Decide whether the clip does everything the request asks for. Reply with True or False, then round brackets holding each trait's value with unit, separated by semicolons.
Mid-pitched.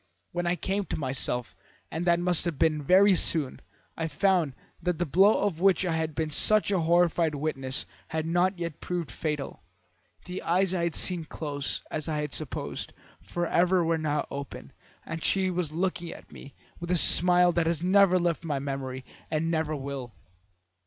True (165 Hz)